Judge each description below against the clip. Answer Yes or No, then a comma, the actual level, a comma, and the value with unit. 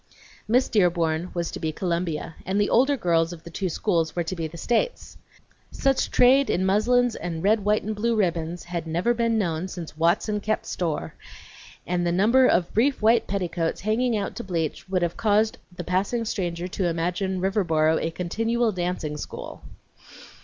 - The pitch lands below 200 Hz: Yes, medium, 185 Hz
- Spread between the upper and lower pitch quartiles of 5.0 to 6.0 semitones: No, average, 4.4 semitones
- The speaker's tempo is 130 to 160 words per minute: No, average, 180 wpm